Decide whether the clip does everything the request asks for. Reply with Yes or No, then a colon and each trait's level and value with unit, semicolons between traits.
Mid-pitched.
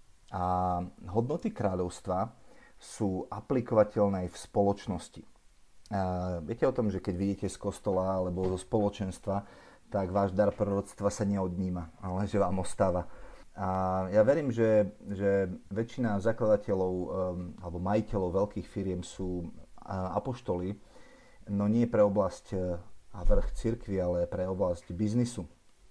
No: low, 100 Hz